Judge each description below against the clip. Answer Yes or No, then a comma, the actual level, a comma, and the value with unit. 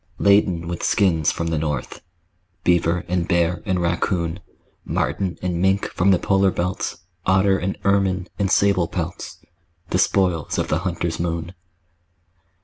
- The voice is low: Yes, very low, 90 Hz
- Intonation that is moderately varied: No, narrow, 2.3 semitones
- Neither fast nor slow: Yes, average, 145 wpm